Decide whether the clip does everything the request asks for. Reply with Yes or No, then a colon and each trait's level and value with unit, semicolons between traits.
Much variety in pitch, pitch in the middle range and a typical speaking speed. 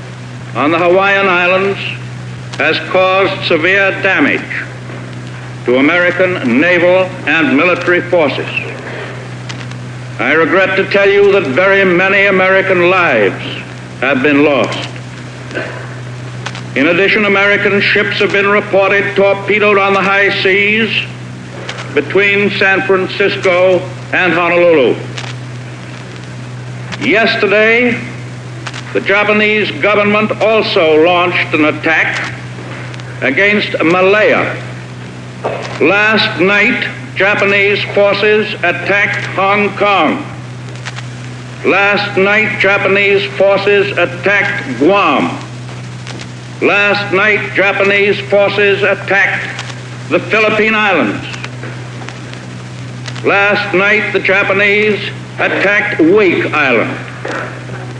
No: wide, 8.4 semitones; medium, 180 Hz; slow, 85 wpm